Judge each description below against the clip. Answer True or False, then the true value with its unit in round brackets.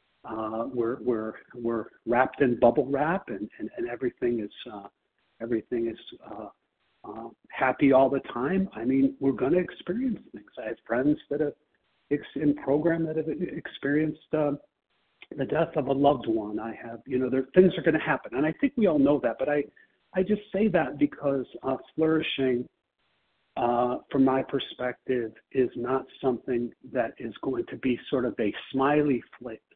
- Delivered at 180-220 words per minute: True (185 wpm)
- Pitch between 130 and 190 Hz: True (135 Hz)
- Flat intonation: False (4.0 semitones)